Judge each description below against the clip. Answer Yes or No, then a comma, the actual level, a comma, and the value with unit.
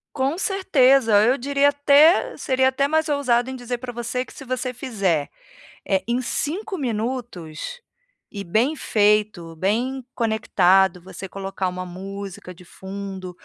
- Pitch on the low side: No, high, 235 Hz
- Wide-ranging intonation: Yes, wide, 5.8 semitones